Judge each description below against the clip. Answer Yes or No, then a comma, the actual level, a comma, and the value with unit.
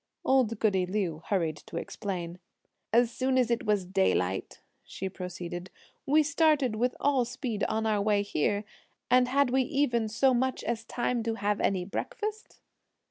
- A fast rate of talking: No, average, 160 wpm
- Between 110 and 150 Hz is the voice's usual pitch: No, high, 225 Hz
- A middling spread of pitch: Yes, average, 4.9 semitones